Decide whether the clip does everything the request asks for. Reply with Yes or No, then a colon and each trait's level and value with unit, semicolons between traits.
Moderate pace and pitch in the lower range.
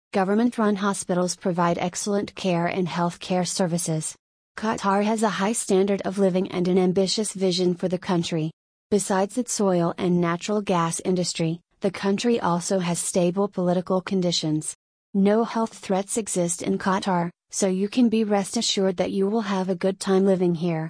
No: average, 170 wpm; high, 190 Hz